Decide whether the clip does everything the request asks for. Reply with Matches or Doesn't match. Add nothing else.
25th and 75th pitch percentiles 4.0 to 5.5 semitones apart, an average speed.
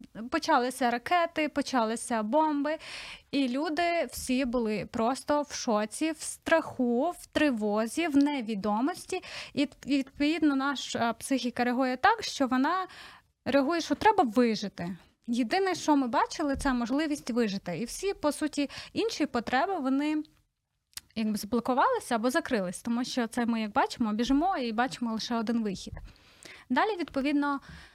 Matches